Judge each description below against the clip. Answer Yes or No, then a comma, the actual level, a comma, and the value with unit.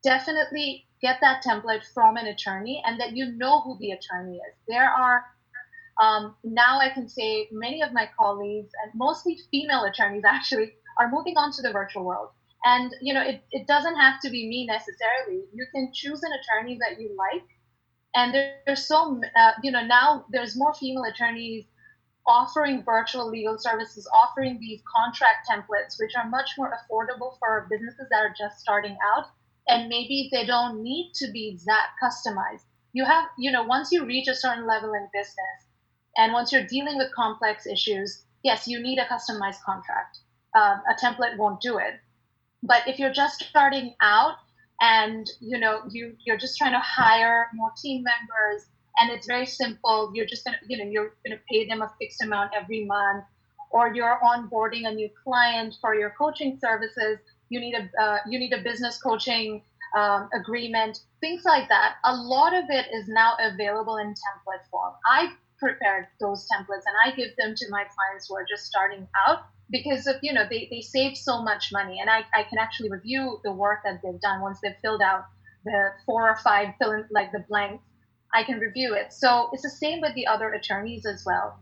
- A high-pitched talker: Yes, high, 235 Hz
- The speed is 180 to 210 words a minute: Yes, average, 195 wpm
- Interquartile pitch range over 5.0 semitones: No, average, 3.5 semitones